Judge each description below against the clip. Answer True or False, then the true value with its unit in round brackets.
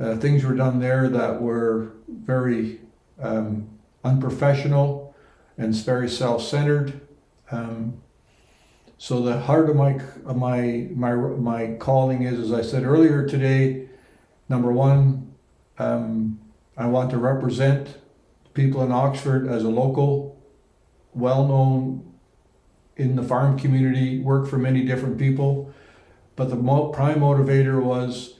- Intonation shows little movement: True (2.3 semitones)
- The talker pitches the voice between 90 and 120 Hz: False (130 Hz)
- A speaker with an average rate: False (130 wpm)